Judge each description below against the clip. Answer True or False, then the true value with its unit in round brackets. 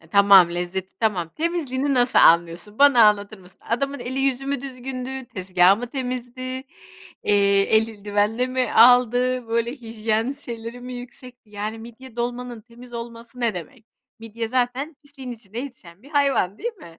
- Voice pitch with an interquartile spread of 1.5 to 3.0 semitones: False (3.5 semitones)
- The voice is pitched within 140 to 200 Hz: False (235 Hz)